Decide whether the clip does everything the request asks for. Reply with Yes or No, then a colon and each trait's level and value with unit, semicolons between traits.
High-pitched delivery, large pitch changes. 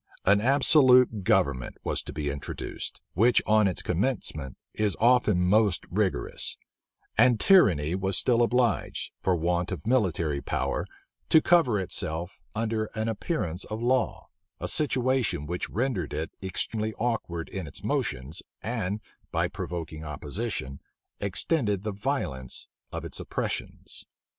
No: low, 100 Hz; wide, 5.9 semitones